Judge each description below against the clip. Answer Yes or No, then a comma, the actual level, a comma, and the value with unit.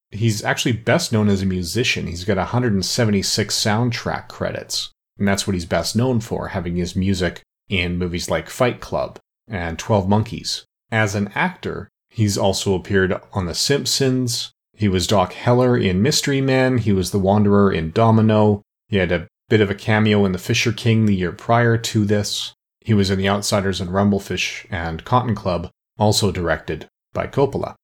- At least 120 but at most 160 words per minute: No, average, 175 wpm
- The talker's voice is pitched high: No, low, 105 Hz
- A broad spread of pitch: No, average, 3.2 semitones